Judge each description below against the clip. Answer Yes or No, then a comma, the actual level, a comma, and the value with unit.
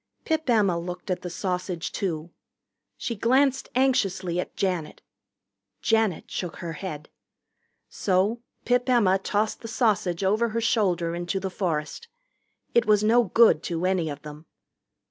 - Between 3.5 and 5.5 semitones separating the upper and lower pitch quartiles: Yes, average, 4.7 semitones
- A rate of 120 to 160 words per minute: Yes, average, 145 wpm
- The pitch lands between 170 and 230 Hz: Yes, high, 190 Hz